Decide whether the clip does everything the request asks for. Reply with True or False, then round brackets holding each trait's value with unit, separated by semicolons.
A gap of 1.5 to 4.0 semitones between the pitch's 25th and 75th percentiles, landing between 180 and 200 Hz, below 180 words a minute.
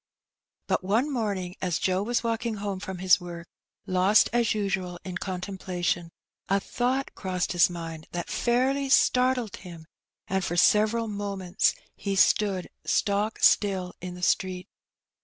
True (3.1 semitones; 190 Hz; 140 wpm)